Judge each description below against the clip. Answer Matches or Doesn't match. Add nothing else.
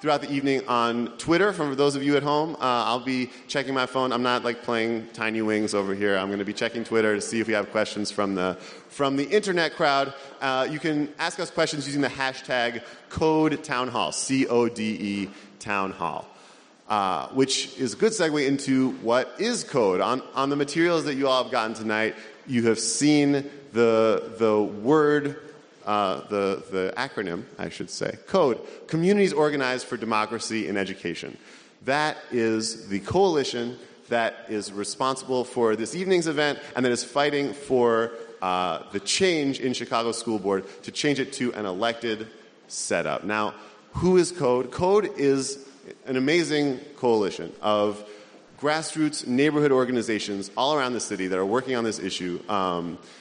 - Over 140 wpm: Matches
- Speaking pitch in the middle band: Doesn't match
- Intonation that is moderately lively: Matches